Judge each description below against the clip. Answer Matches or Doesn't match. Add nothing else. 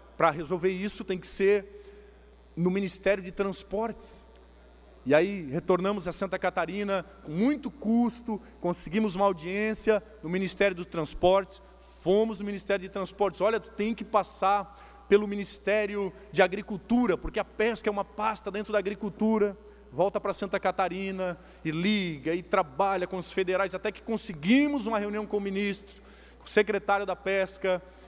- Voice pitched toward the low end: Doesn't match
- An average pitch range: Doesn't match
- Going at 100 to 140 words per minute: Doesn't match